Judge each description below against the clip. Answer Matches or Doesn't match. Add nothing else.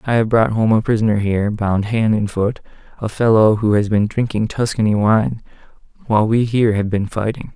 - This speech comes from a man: Matches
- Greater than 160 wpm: Matches